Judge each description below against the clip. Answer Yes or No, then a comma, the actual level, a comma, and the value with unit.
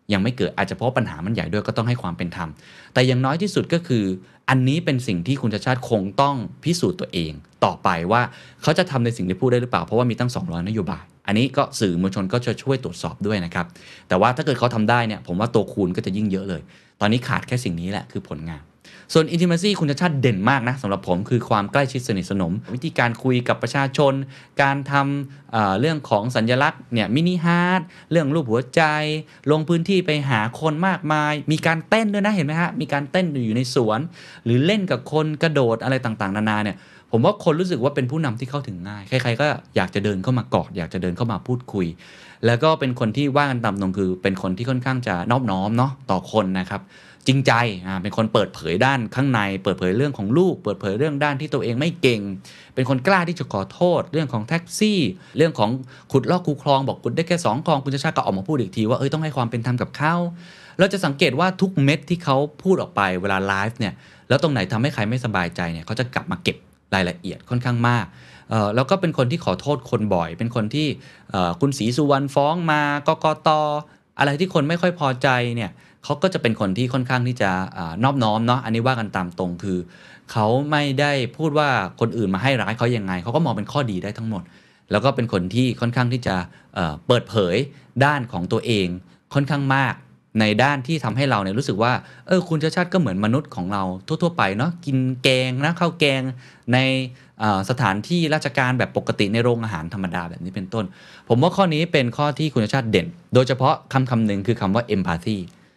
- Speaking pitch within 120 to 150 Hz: Yes, low, 125 Hz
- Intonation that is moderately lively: No, wide, 6.1 semitones